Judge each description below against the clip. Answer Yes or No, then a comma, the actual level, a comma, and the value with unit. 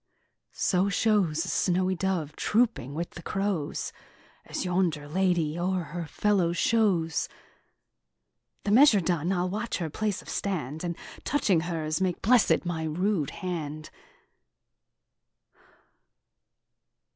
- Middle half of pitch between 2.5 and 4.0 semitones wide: Yes, average, 3.4 semitones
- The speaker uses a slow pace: Yes, slow, 110 wpm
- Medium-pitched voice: Yes, medium, 180 Hz